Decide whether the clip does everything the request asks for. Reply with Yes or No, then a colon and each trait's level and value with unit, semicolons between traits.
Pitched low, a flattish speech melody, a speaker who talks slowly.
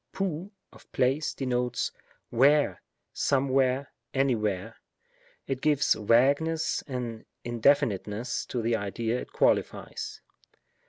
No: low, 130 Hz; average, 3.4 semitones; slow, 95 wpm